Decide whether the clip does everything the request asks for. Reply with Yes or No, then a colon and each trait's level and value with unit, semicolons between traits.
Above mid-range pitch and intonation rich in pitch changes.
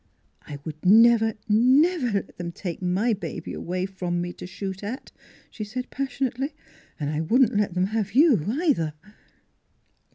Yes: high, 210 Hz; wide, 5.7 semitones